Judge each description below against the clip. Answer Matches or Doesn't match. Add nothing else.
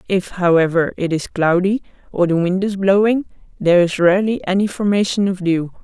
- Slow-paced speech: Doesn't match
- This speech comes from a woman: Matches